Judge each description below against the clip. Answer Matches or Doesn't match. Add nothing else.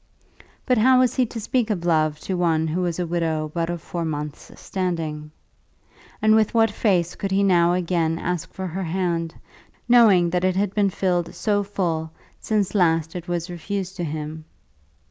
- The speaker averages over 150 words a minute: Matches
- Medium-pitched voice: Matches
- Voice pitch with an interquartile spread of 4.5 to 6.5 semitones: Doesn't match